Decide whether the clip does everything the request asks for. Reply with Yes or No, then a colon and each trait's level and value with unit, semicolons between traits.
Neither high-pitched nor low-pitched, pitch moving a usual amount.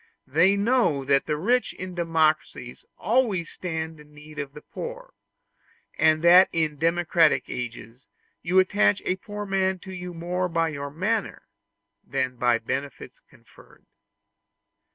Yes: medium, 165 Hz; average, 4.1 semitones